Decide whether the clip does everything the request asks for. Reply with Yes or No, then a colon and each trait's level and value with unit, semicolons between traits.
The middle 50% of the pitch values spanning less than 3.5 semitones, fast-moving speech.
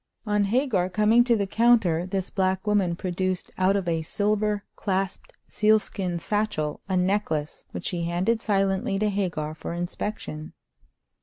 No: average, 3.0 semitones; average, 145 wpm